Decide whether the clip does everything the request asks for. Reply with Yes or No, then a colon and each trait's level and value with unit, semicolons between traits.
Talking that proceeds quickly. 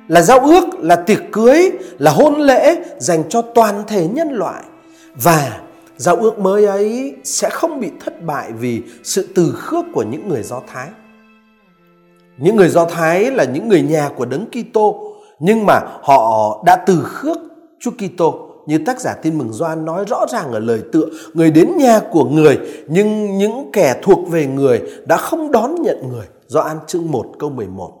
No: average, 185 wpm